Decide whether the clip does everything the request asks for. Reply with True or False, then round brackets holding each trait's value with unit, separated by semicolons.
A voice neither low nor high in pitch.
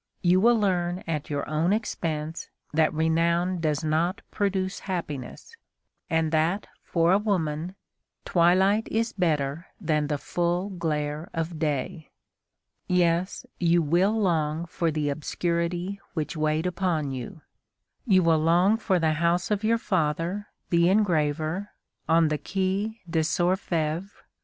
True (170 Hz)